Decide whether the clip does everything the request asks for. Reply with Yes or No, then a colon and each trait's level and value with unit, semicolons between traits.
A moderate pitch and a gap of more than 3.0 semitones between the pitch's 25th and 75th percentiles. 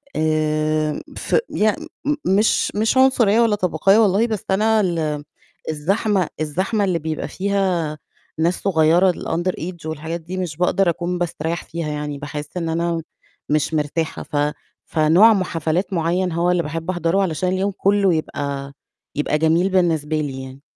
Yes: medium, 170 Hz; average, 3.5 semitones